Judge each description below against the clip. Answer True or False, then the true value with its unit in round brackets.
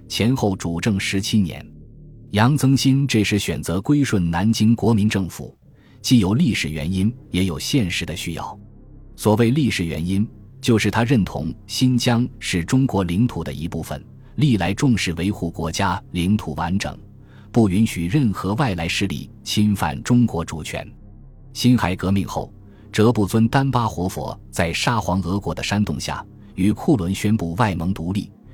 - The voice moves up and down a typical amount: True (4.6 semitones)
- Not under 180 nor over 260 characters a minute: True (240 characters per minute)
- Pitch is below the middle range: True (105 Hz)